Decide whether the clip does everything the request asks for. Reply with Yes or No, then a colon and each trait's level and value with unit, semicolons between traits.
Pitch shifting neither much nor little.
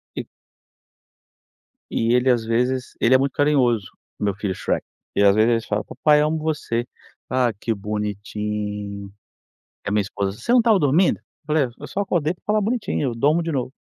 No: wide, 6.3 semitones